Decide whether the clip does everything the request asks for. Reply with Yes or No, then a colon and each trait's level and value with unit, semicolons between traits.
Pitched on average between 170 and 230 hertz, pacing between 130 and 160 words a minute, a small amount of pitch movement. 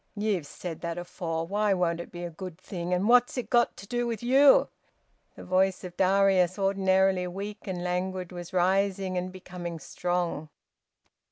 No: medium, 185 Hz; average, 170 wpm; narrow, 2.0 semitones